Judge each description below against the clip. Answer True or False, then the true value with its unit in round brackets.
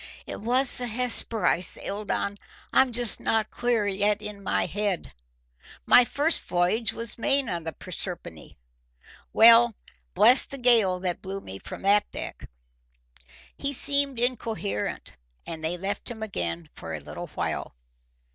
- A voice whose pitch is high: True (210 Hz)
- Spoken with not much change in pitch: False (4.6 semitones)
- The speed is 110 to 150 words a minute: True (145 wpm)